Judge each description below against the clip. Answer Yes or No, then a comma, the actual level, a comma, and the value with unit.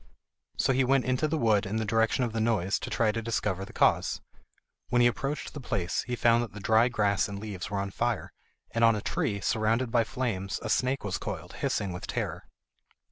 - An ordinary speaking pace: No, fast, 220 wpm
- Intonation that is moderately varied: Yes, average, 3.1 semitones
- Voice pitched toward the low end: Yes, low, 115 Hz